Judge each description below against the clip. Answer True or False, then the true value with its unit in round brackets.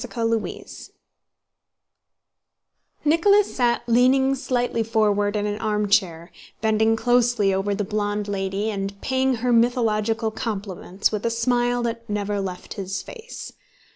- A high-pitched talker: True (220 Hz)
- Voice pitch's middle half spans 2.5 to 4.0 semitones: True (3.0 semitones)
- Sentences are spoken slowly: True (125 wpm)